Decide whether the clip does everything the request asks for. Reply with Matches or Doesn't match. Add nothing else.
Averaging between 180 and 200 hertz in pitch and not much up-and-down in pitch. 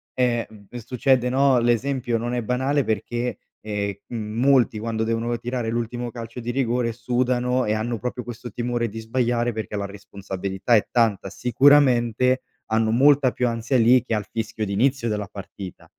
Doesn't match